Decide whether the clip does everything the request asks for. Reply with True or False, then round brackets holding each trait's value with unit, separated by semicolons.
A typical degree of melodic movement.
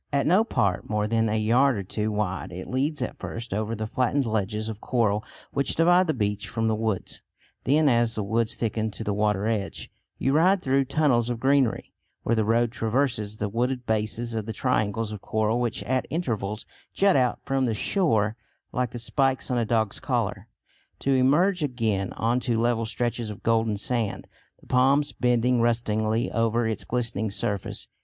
True (3.1 semitones)